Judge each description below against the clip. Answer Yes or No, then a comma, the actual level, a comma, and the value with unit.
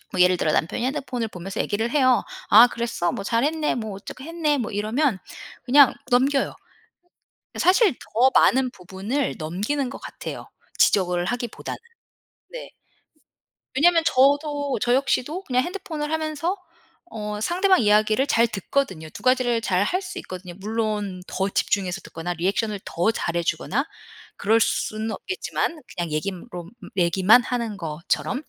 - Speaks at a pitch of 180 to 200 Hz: No, high, 230 Hz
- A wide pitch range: Yes, wide, 6.4 semitones